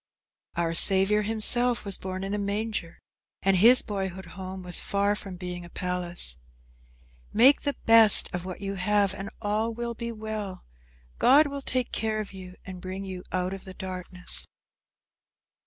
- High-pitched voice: Yes, high, 195 Hz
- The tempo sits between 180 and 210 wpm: No, average, 165 wpm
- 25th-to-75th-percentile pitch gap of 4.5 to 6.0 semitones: No, average, 2.9 semitones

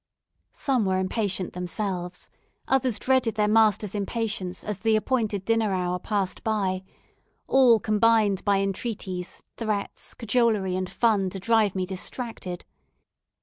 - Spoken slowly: Yes, slow, 125 wpm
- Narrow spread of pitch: No, average, 3.2 semitones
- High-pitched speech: Yes, high, 205 Hz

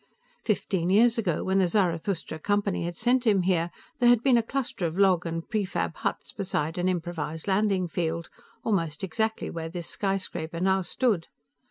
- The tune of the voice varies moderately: Yes, average, 4.0 semitones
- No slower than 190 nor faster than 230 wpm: No, average, 170 wpm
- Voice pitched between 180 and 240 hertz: Yes, medium, 185 Hz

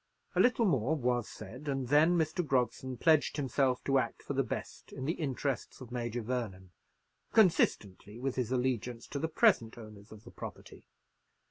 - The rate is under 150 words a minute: No, average, 170 wpm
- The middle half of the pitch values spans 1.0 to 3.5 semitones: No, average, 3.9 semitones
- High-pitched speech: No, low, 130 Hz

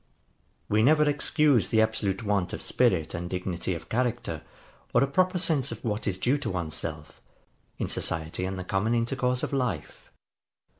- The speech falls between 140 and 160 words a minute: No, average, 180 wpm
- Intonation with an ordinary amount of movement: No, wide, 6.0 semitones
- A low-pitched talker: Yes, low, 110 Hz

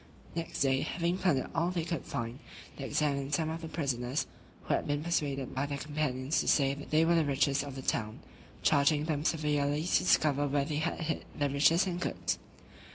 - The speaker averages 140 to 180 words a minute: No, average, 200 wpm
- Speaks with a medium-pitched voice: Yes, medium, 145 Hz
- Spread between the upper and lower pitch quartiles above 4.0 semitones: No, narrow, 2.6 semitones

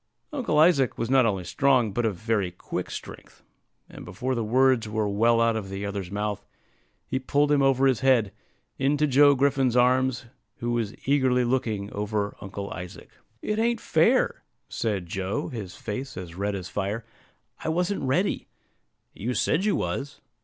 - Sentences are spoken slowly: No, average, 165 wpm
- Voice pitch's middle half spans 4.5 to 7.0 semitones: Yes, average, 4.8 semitones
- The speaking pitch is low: Yes, low, 120 Hz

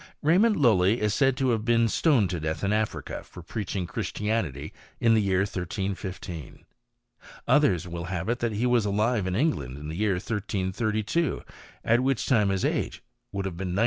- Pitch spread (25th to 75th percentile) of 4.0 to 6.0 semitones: Yes, average, 4.3 semitones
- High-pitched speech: No, low, 105 Hz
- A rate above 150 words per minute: Yes, average, 180 wpm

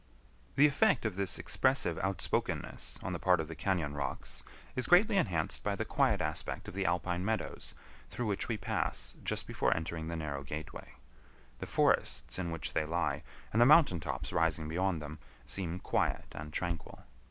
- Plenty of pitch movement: No, average, 3.8 semitones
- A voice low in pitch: Yes, very low, 85 Hz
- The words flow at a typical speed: Yes, average, 175 wpm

